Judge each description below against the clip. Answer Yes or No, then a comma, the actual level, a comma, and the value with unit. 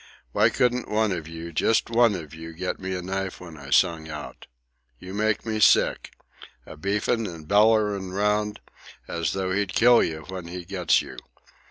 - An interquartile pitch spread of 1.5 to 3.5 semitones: No, average, 4.1 semitones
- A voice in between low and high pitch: No, very low, 95 Hz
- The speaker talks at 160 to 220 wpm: Yes, average, 180 wpm